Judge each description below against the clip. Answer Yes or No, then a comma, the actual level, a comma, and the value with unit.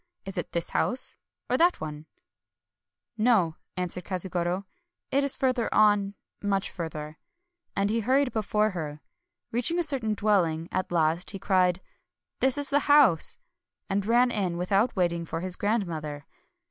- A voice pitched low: No, high, 195 Hz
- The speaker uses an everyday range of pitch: No, wide, 6.0 semitones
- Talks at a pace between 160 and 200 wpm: Yes, average, 175 wpm